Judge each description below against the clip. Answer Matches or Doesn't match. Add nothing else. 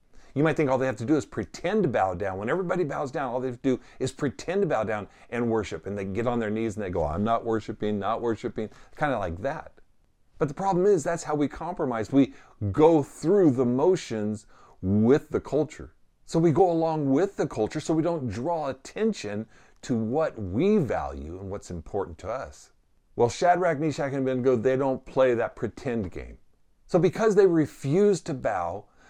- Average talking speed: Doesn't match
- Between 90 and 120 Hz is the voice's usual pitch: Doesn't match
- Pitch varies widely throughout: Matches